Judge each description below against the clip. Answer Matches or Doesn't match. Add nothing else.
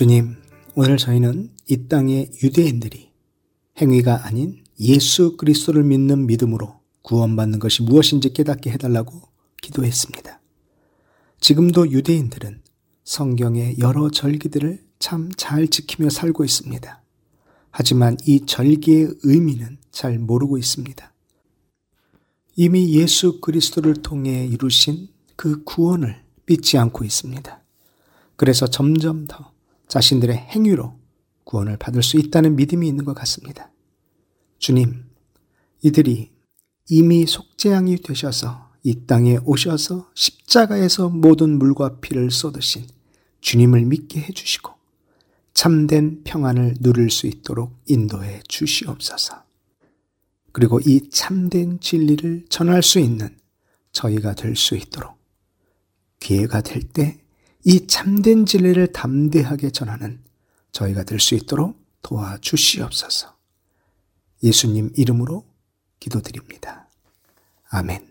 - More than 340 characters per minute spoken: Doesn't match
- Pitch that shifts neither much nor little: Matches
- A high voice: Doesn't match